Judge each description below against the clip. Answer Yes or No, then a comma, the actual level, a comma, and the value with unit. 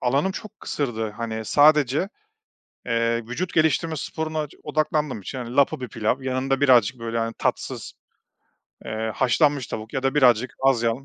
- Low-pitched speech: Yes, low, 130 Hz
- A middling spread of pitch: Yes, average, 4.2 semitones